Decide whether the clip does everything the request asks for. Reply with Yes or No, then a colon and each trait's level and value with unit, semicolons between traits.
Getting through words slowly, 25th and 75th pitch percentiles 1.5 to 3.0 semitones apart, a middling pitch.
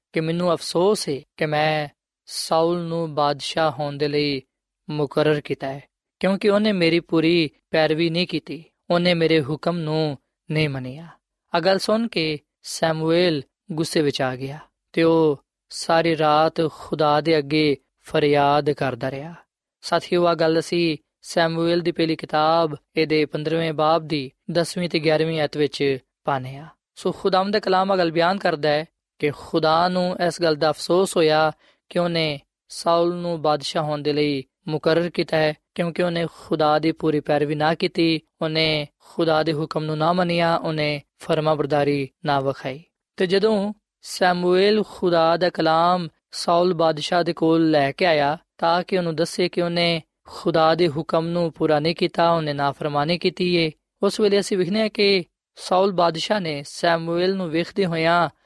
No: average, 155 wpm; narrow, 2.4 semitones; medium, 165 Hz